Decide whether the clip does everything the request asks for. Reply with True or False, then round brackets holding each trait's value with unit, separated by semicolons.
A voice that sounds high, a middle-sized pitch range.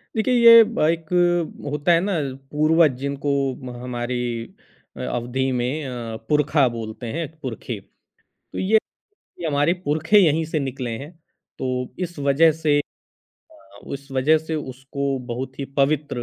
False (145 Hz; 3.8 semitones)